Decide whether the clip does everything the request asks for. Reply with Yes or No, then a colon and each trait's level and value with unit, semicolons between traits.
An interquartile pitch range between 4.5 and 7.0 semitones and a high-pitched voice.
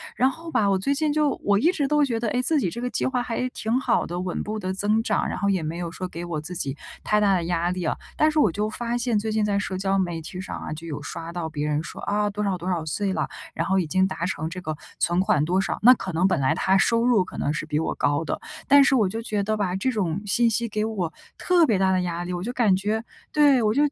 Yes: average, 4.8 semitones; high, 195 Hz